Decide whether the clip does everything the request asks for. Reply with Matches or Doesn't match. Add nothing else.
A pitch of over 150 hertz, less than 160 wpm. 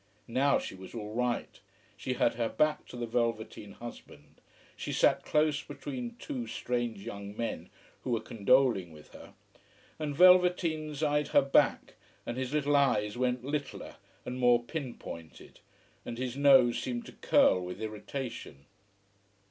Doesn't match